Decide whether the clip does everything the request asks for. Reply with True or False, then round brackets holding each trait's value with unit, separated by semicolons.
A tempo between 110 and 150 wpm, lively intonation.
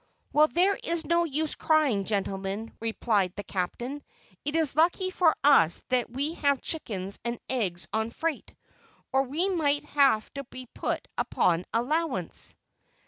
True (145 wpm; 6.5 semitones)